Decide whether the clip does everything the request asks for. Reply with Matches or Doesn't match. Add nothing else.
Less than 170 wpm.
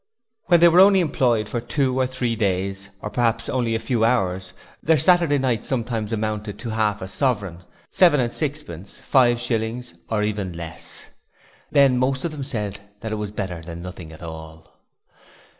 Doesn't match